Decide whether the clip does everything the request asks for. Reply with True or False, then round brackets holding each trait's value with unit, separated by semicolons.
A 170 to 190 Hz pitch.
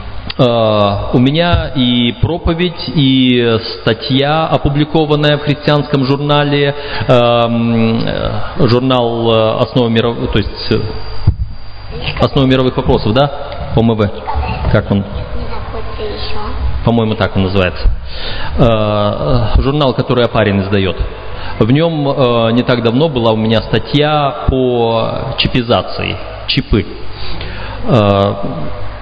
False (115 Hz)